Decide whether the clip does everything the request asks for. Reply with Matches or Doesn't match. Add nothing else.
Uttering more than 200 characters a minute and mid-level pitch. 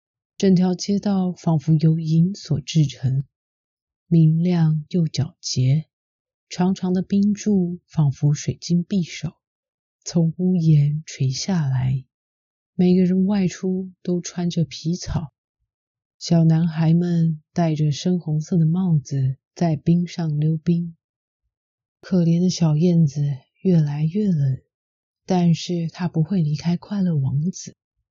Doesn't match